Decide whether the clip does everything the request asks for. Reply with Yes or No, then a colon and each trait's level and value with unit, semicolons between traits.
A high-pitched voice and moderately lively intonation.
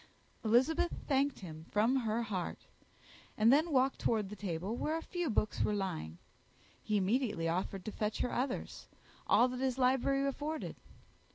Yes: high, 235 Hz; average, 4.7 semitones